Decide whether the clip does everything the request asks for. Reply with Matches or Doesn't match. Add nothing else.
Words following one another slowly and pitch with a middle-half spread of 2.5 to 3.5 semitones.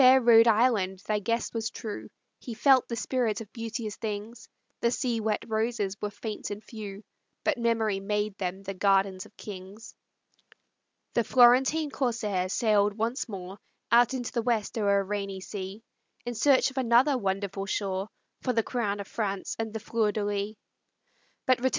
Doesn't match